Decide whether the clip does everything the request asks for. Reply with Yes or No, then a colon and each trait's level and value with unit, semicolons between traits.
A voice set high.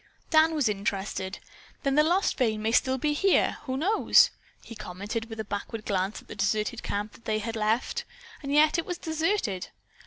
Yes: high, 230 Hz